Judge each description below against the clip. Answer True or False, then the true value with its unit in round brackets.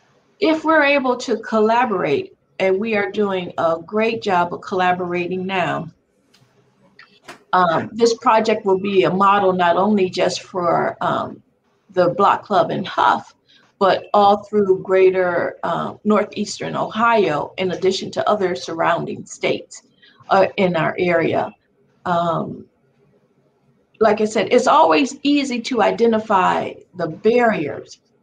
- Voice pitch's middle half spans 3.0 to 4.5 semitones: True (3.3 semitones)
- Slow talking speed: True (130 wpm)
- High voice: True (200 Hz)